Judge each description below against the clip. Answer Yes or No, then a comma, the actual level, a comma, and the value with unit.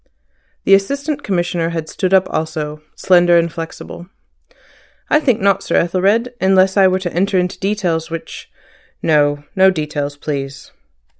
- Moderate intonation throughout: Yes, average, 3.2 semitones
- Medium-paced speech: Yes, average, 145 wpm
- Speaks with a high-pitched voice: No, medium, 180 Hz